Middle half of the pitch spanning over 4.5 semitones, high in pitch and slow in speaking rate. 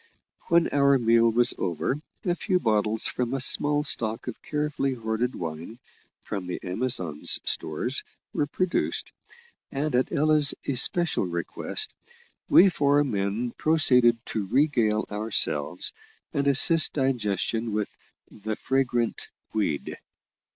No: average, 5.0 semitones; low, 120 Hz; slow, 120 wpm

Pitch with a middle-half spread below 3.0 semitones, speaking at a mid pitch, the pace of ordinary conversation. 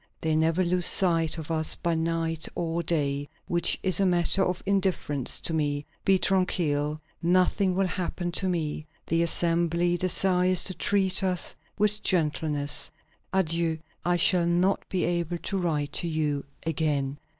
Yes: narrow, 2.6 semitones; medium, 170 Hz; average, 150 wpm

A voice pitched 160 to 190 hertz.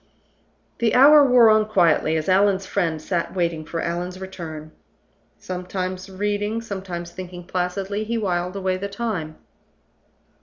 Yes: medium, 185 Hz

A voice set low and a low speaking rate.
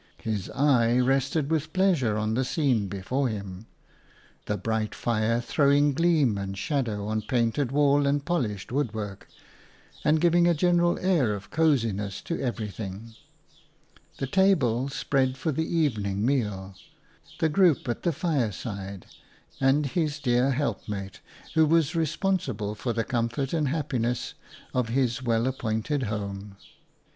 No: low, 125 Hz; average, 150 wpm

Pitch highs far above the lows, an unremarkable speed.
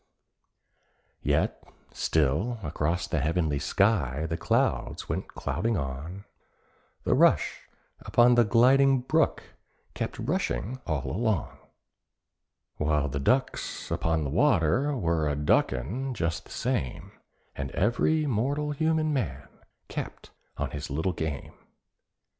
No: wide, 8.8 semitones; slow, 115 wpm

